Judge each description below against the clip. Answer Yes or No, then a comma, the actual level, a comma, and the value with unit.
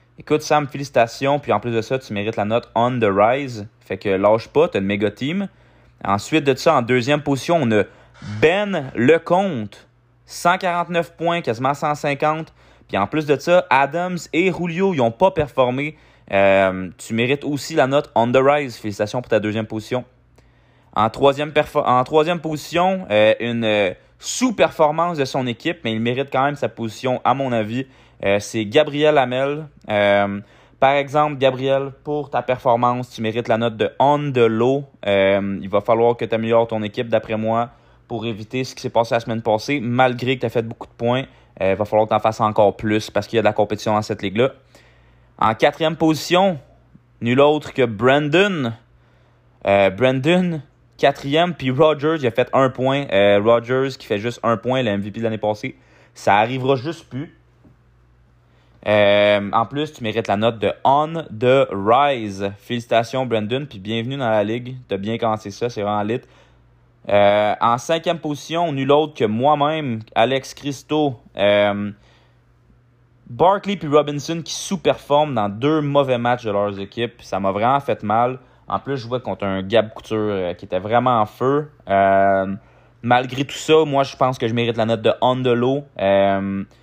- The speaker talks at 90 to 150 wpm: No, average, 185 wpm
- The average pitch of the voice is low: Yes, low, 120 Hz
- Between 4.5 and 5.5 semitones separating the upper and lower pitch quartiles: Yes, average, 5.0 semitones